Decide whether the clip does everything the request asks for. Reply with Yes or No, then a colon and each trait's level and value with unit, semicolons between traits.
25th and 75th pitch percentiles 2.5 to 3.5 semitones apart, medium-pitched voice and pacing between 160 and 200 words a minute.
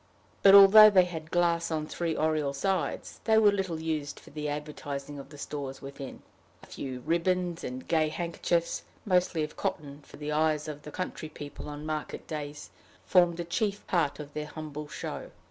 Yes: average, 3.0 semitones; medium, 155 Hz; average, 180 wpm